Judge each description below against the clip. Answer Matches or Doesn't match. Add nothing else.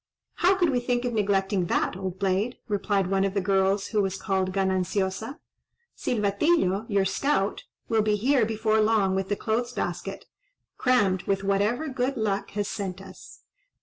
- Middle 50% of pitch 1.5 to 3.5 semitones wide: Matches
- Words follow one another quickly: Doesn't match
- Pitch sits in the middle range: Doesn't match